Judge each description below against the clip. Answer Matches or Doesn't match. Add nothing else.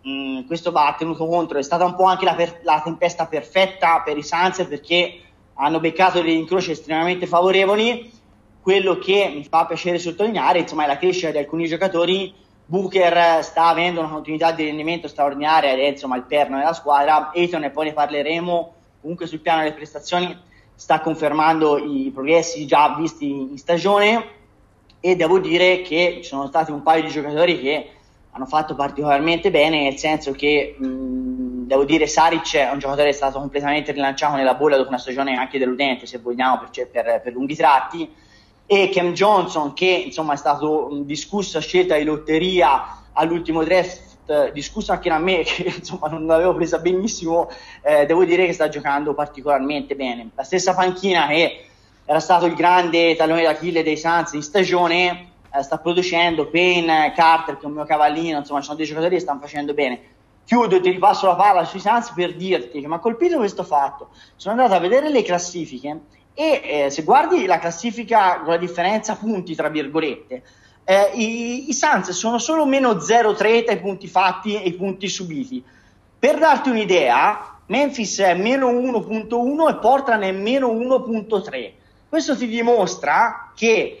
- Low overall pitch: Doesn't match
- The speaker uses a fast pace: Matches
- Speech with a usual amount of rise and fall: Matches